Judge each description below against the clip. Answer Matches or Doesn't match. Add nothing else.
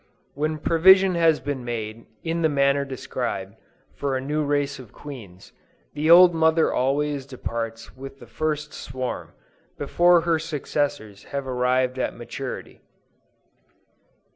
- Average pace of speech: Doesn't match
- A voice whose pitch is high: Doesn't match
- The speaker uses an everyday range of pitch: Matches